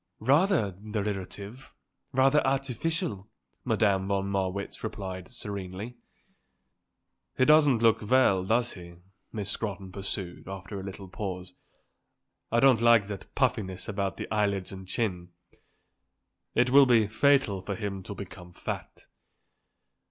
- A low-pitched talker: Yes, low, 100 Hz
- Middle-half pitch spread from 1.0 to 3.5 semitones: No, average, 4.1 semitones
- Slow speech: Yes, slow, 120 wpm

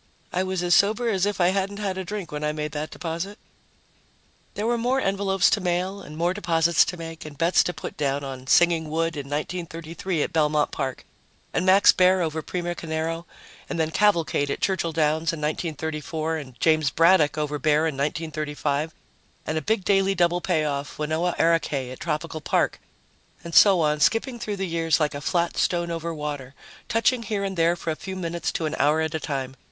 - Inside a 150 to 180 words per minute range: No, average, 200 wpm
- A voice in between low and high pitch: Yes, medium, 165 Hz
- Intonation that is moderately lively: Yes, average, 3.4 semitones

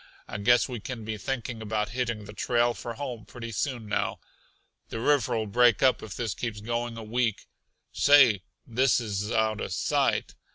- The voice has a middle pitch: No, low, 115 Hz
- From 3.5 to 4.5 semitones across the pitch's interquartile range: No, narrow, 2.4 semitones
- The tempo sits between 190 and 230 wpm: No, average, 175 wpm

